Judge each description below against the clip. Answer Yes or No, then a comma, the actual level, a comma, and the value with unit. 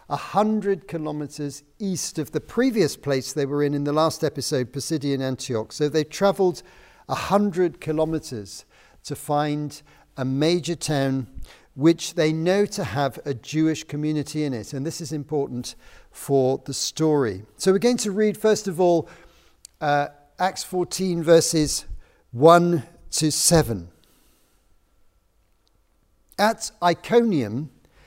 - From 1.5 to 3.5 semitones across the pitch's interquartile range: No, average, 4.0 semitones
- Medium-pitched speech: Yes, medium, 150 Hz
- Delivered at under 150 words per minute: Yes, slow, 135 wpm